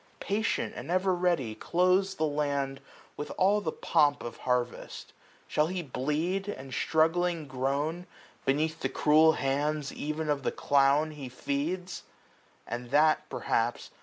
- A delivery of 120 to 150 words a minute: Yes, average, 140 wpm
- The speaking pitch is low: No, medium, 150 Hz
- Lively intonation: No, average, 4.1 semitones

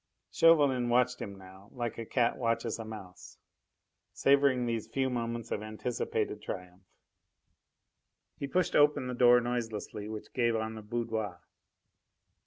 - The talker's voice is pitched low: Yes, low, 115 Hz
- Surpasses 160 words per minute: No, slow, 135 wpm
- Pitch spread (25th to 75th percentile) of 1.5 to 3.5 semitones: Yes, narrow, 2.6 semitones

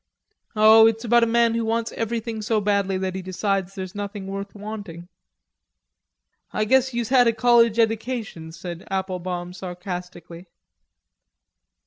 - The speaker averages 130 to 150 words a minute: Yes, slow, 135 wpm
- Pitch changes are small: No, average, 3.4 semitones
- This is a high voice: Yes, high, 205 Hz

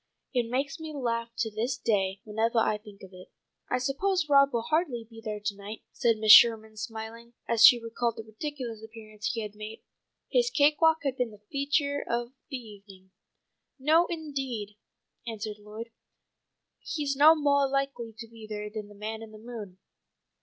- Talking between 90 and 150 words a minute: No, average, 180 wpm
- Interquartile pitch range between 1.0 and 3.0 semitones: No, average, 4.4 semitones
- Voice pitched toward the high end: Yes, high, 230 Hz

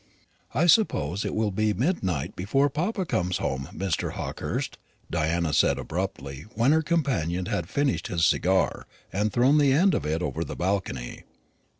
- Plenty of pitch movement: Yes, wide, 9.0 semitones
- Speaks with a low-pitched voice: Yes, very low, 95 Hz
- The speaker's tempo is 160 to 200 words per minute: Yes, average, 165 wpm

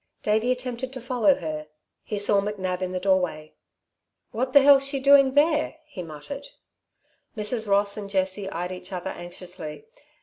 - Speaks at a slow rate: No, average, 160 wpm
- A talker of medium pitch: No, high, 205 Hz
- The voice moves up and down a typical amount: No, wide, 5.9 semitones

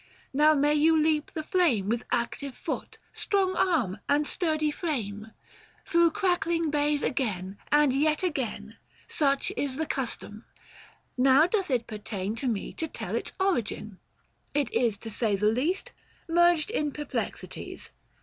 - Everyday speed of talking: Yes, average, 150 wpm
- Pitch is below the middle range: No, very high, 290 Hz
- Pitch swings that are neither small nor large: No, wide, 5.8 semitones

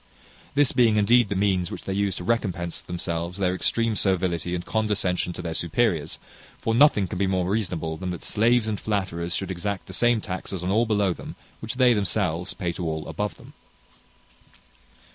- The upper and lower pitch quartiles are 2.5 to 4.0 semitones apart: Yes, average, 3.7 semitones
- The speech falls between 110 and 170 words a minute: No, average, 190 wpm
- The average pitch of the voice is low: Yes, very low, 95 Hz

